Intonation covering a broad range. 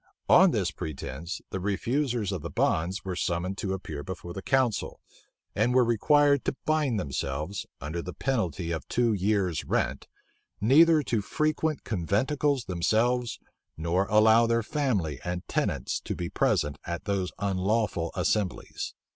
Yes: wide, 5.9 semitones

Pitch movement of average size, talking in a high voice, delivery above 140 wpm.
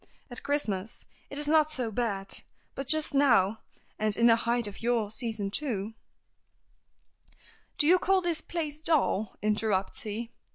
No: wide, 5.7 semitones; high, 235 Hz; average, 155 wpm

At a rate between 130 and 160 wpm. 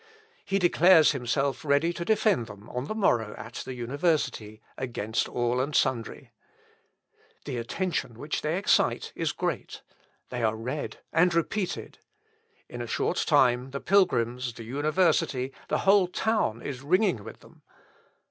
Yes: average, 145 wpm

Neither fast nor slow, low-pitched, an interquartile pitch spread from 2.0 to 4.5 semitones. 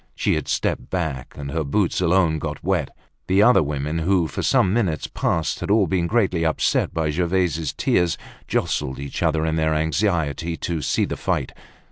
Yes: average, 180 wpm; very low, 80 Hz; average, 2.9 semitones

